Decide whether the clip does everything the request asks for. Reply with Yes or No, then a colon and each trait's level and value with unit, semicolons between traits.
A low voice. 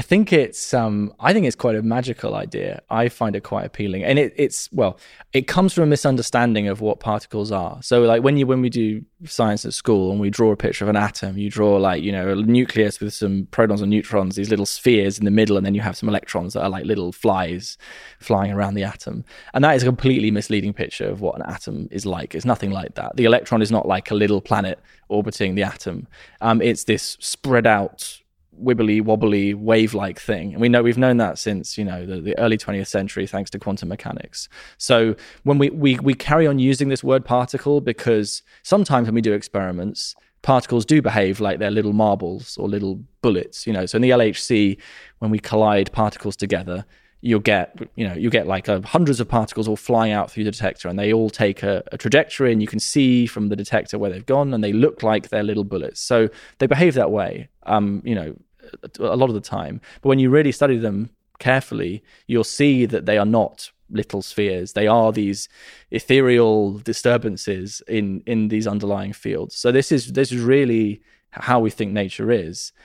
Yes: low, 110 Hz